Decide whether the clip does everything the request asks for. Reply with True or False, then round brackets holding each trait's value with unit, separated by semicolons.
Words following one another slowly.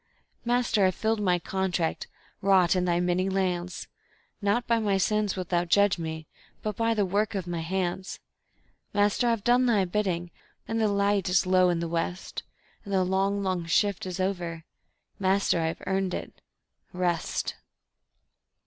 False (160 wpm)